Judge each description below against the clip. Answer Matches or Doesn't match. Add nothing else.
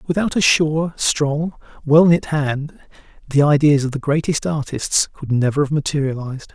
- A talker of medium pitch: Matches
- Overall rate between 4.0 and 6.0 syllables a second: Matches